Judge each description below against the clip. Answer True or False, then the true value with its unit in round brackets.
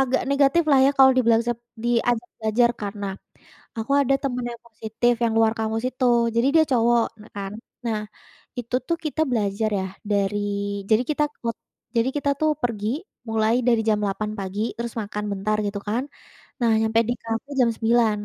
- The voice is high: True (230 Hz)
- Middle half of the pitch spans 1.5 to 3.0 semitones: True (2.4 semitones)